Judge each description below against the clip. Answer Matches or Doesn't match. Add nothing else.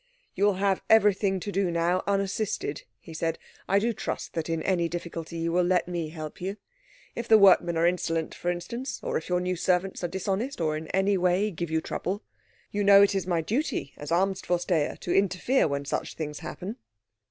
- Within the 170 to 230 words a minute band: Matches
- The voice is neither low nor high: Matches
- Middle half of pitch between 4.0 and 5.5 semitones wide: Doesn't match